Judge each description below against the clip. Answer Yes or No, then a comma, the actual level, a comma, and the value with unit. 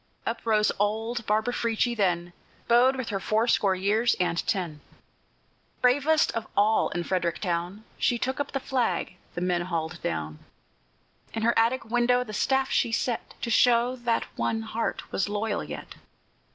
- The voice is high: Yes, high, 220 Hz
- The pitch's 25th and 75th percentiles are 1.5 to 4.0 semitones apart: No, average, 4.4 semitones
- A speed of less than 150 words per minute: No, average, 160 wpm